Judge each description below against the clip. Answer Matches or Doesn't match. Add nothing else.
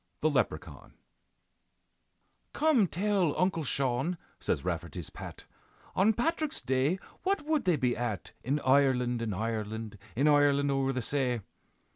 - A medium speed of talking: Doesn't match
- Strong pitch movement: Matches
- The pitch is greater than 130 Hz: Matches